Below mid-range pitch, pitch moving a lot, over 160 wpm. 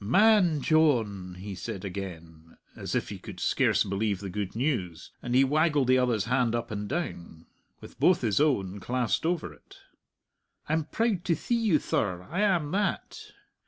Yes: low, 120 Hz; wide, 8.3 semitones; average, 170 wpm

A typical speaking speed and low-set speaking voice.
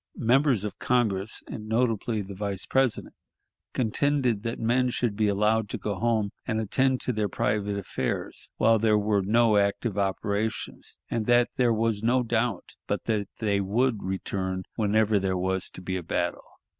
Yes: average, 170 wpm; low, 110 Hz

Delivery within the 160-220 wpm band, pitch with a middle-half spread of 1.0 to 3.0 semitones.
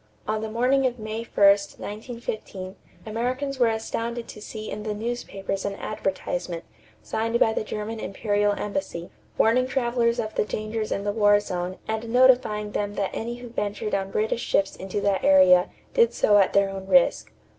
Yes: average, 175 wpm; average, 2.7 semitones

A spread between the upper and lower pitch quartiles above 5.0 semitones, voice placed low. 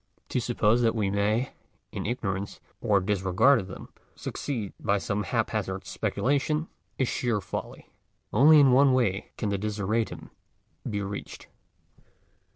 No: average, 3.9 semitones; low, 105 Hz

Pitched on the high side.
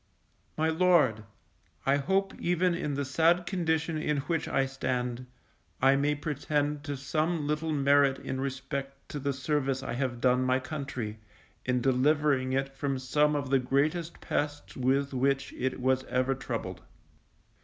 No: medium, 140 Hz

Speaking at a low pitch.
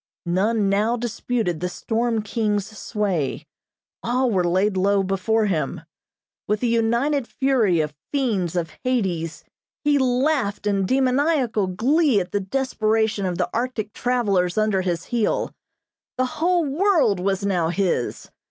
No: high, 215 Hz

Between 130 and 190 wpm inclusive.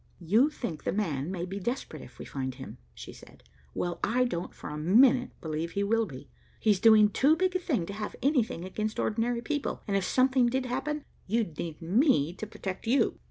No: fast, 205 wpm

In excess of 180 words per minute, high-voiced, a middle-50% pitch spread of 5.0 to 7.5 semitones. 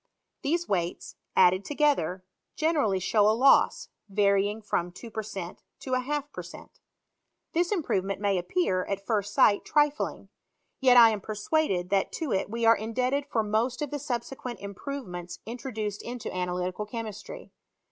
No: average, 165 wpm; high, 220 Hz; average, 5.3 semitones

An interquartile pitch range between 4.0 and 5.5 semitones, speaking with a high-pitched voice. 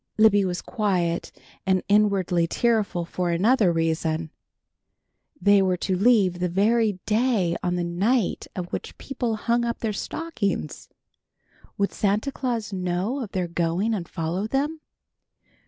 Yes: average, 4.3 semitones; high, 200 Hz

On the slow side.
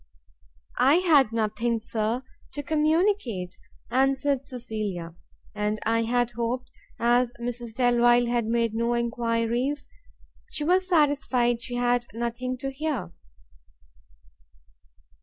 Yes: slow, 100 wpm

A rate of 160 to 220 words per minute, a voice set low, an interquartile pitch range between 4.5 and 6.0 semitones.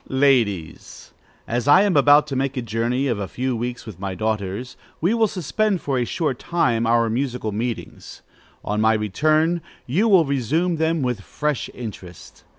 Yes: average, 175 wpm; low, 125 Hz; wide, 5.5 semitones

